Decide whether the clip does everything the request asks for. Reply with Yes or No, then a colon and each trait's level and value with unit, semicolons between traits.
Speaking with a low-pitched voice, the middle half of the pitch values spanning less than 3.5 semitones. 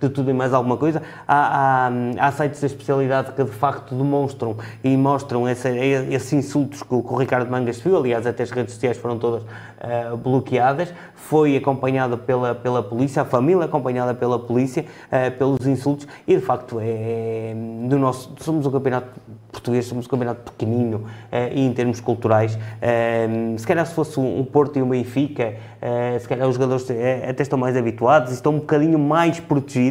Yes: low, 130 Hz; average, 2.7 semitones